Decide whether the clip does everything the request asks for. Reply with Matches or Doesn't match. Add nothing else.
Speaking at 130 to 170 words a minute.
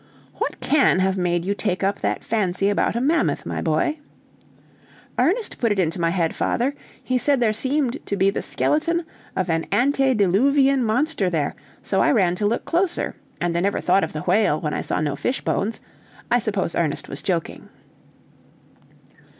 Doesn't match